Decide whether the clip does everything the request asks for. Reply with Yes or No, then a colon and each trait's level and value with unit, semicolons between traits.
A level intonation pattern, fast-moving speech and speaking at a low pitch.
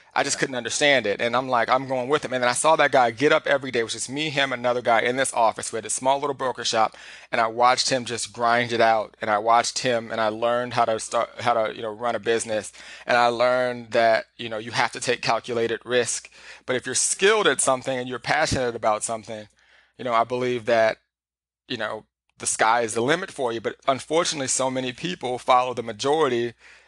Yes: narrow, 2.1 semitones; fast, 240 wpm; low, 120 Hz